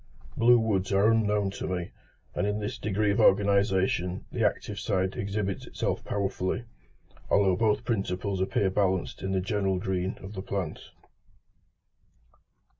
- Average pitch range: No, narrow, 1.6 semitones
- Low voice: Yes, low, 100 Hz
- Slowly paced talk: No, average, 145 wpm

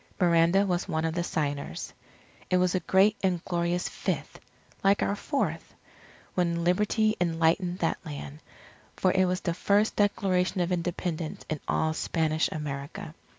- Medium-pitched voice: Yes, medium, 175 Hz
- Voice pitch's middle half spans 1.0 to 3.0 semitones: Yes, narrow, 2.5 semitones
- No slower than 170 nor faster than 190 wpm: No, average, 150 wpm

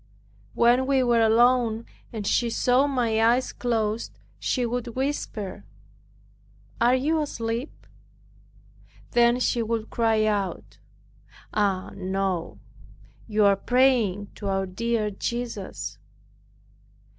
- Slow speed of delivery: Yes, slow, 105 wpm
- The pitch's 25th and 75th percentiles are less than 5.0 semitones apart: Yes, average, 2.9 semitones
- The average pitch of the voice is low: No, high, 230 Hz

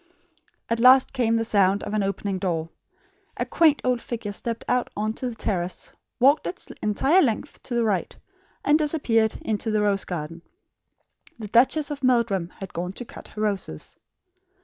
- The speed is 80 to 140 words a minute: No, average, 170 wpm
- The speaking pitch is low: No, high, 225 Hz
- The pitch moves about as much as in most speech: Yes, average, 4.2 semitones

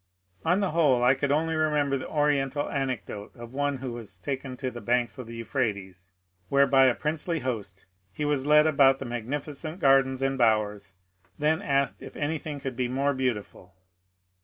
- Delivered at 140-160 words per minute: No, average, 180 wpm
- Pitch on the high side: No, low, 135 Hz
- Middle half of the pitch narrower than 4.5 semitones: Yes, average, 3.5 semitones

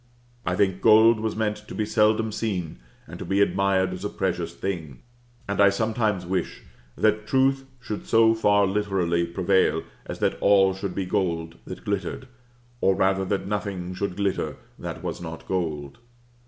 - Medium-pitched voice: No, low, 100 Hz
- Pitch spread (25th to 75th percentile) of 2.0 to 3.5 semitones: Yes, average, 2.8 semitones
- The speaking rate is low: No, average, 165 wpm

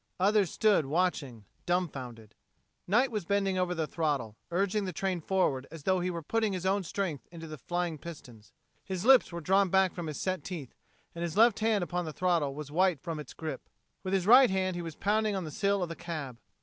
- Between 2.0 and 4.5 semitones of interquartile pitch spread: Yes, average, 3.7 semitones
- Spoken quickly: Yes, fast, 215 wpm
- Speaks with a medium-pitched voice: Yes, medium, 180 Hz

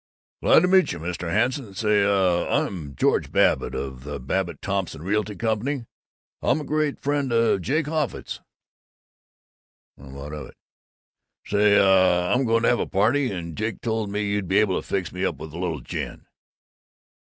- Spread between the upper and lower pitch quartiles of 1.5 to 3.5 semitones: No, average, 4.8 semitones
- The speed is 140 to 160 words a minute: No, average, 175 wpm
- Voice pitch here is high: No, low, 100 Hz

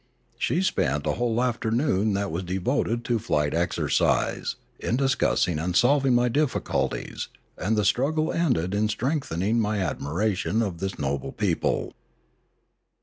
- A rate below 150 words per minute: Yes, average, 140 wpm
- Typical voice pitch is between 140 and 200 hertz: No, low, 110 Hz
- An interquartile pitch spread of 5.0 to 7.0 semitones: Yes, wide, 5.4 semitones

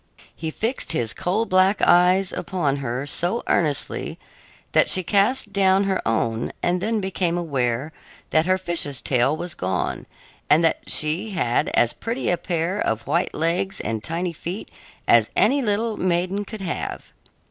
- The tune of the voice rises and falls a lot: No, average, 4.6 semitones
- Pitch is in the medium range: Yes, medium, 175 Hz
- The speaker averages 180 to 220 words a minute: No, average, 160 wpm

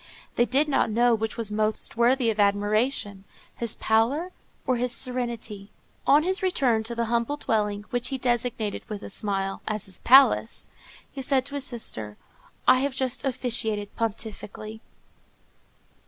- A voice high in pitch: Yes, high, 235 Hz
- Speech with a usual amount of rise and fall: Yes, average, 3.3 semitones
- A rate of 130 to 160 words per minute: Yes, average, 155 wpm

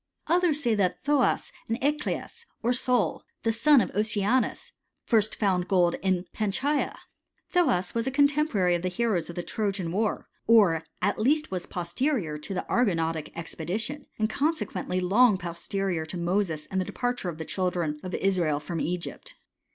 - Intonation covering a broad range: Yes, wide, 5.9 semitones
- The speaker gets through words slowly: No, average, 160 wpm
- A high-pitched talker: Yes, high, 200 Hz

